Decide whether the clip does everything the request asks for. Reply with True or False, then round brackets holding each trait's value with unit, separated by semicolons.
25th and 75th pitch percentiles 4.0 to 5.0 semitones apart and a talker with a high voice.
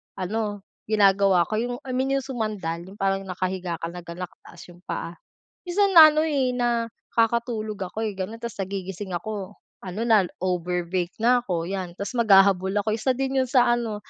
True (4.3 semitones; 205 Hz)